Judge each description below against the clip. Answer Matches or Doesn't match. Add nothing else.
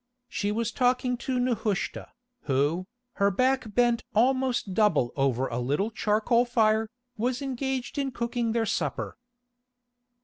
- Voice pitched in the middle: Doesn't match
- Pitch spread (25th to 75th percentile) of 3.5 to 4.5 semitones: Matches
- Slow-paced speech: Matches